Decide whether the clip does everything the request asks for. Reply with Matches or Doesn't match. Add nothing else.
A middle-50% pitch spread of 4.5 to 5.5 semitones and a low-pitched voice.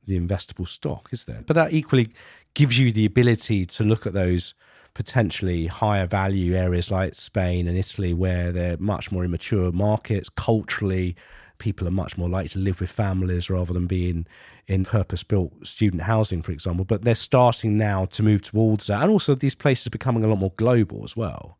Doesn't match